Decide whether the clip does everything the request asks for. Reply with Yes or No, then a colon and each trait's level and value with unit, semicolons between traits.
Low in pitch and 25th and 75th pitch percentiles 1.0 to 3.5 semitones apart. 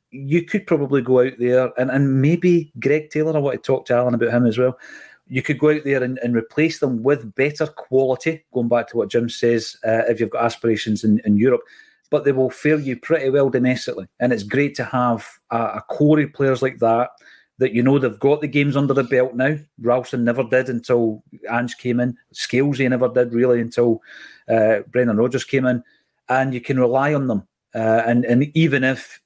Yes: low, 130 Hz; average, 2.8 semitones